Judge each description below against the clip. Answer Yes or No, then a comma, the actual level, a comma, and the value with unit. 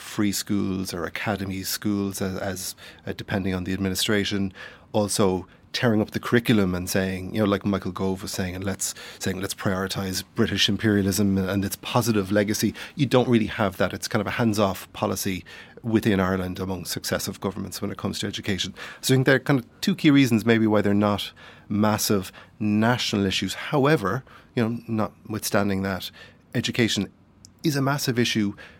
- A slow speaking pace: No, average, 180 wpm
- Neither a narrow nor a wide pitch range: No, narrow, 2.3 semitones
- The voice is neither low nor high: No, low, 100 Hz